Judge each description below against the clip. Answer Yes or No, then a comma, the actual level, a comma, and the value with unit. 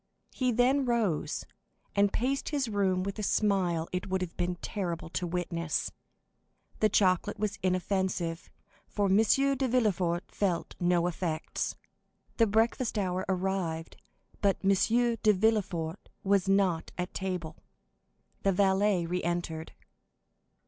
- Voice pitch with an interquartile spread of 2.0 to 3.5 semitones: Yes, average, 3.2 semitones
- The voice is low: No, high, 190 Hz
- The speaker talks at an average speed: No, slow, 130 wpm